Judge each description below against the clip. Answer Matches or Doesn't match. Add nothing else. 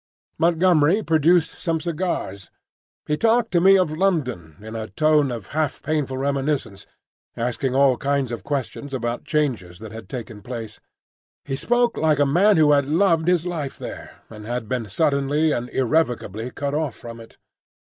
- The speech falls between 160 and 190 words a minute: Matches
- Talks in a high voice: Doesn't match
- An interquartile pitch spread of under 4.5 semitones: Doesn't match